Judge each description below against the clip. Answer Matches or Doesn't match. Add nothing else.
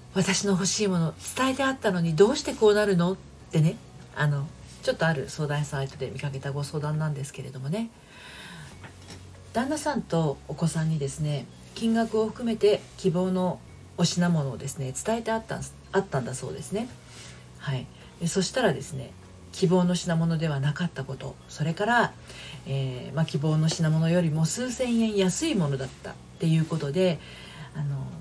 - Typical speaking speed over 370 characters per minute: Doesn't match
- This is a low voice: Doesn't match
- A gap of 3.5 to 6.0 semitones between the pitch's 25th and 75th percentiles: Matches